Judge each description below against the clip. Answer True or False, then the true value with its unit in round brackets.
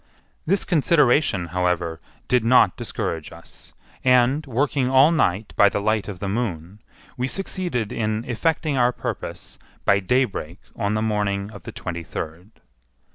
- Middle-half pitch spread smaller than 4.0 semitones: False (5.0 semitones)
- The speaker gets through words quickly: False (145 wpm)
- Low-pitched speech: True (110 Hz)